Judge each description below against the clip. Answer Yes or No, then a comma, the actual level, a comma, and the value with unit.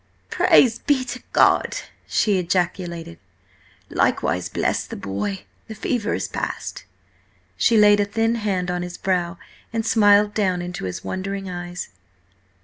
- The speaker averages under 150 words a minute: Yes, average, 140 wpm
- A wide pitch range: No, average, 3.3 semitones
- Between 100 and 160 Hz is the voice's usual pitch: No, high, 190 Hz